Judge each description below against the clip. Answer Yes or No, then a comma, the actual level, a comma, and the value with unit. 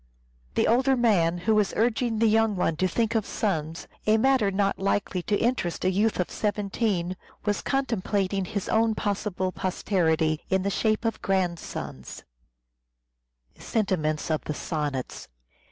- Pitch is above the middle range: Yes, high, 205 Hz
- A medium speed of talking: No, slow, 130 wpm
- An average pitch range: Yes, average, 3.3 semitones